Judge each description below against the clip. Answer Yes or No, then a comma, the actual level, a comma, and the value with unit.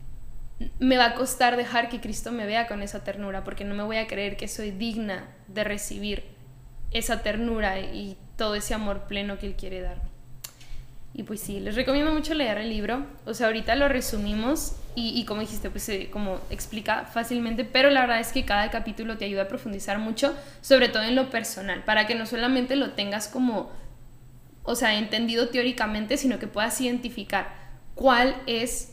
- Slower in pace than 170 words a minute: No, fast, 190 wpm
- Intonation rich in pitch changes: No, average, 3.3 semitones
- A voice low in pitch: No, high, 220 Hz